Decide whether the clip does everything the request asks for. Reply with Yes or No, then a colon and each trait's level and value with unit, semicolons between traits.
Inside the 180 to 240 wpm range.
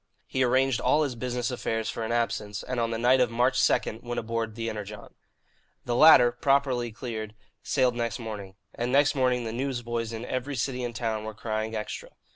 Yes: average, 200 wpm